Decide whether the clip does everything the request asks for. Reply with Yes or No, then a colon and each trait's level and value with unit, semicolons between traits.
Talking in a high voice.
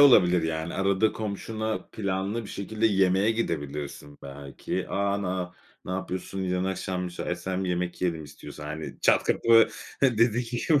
No: very low, 95 Hz